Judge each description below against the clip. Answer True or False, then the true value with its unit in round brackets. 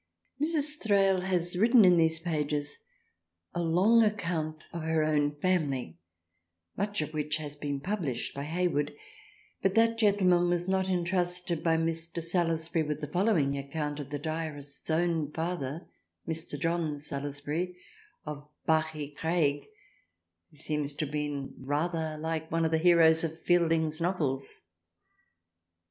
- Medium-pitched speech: True (160 Hz)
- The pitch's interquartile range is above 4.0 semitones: False (3.0 semitones)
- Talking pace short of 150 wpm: True (135 wpm)